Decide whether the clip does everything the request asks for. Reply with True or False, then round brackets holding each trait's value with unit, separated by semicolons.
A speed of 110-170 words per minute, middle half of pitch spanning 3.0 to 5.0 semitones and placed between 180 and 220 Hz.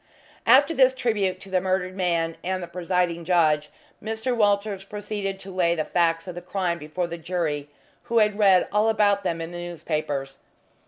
False (180 wpm; 3.3 semitones; 185 Hz)